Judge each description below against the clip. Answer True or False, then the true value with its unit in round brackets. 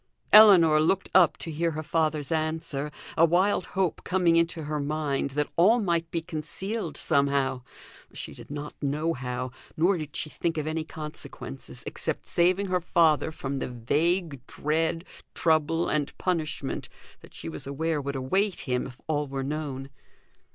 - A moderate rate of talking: True (160 wpm)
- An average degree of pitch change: True (3.0 semitones)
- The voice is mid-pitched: True (155 Hz)